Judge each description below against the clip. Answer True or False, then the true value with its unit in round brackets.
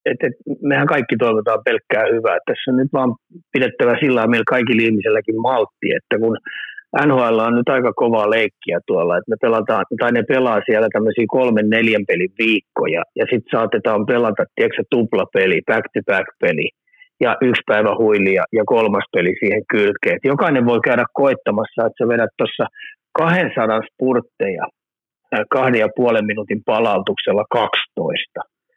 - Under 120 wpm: False (155 wpm)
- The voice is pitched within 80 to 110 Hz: False (130 Hz)